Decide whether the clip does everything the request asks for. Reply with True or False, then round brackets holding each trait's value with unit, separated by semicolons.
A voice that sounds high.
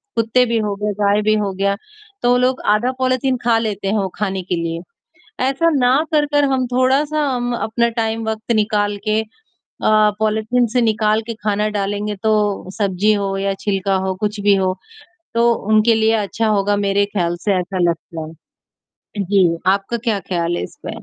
True (210 Hz)